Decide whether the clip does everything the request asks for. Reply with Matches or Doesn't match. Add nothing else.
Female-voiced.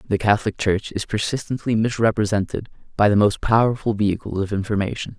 Doesn't match